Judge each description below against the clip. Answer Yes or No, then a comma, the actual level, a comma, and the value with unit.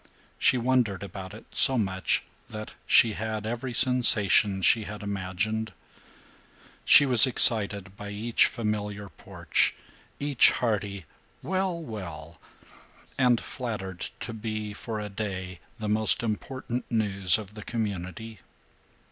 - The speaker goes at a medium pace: No, slow, 120 wpm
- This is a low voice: Yes, low, 110 Hz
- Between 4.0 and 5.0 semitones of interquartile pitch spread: No, average, 2.9 semitones